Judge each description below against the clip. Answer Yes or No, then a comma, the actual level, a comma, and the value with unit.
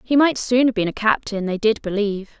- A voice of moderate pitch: No, high, 220 Hz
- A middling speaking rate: No, fast, 250 wpm